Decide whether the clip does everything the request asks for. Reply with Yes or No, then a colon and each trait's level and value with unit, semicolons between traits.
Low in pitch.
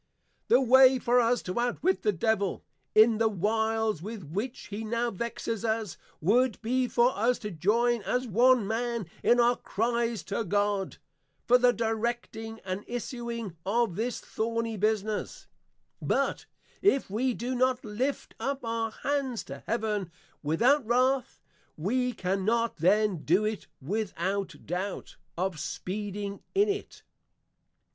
No: high, 225 Hz